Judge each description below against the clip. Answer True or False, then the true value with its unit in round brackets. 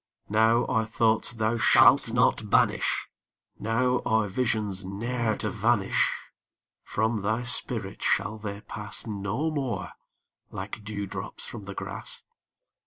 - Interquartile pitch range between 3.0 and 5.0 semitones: False (2.5 semitones)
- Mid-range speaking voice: False (110 Hz)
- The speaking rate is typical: False (125 wpm)